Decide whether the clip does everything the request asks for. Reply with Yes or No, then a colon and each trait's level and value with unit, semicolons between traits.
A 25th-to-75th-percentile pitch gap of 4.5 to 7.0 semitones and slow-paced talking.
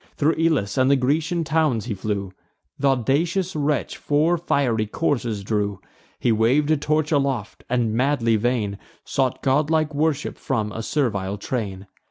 No: wide, 5.6 semitones; average, 150 wpm